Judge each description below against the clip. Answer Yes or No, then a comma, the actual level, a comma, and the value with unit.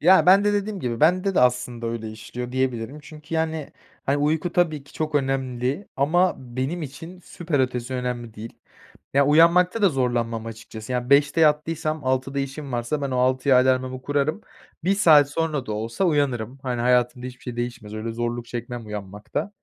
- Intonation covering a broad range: No, average, 4.3 semitones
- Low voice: Yes, low, 130 Hz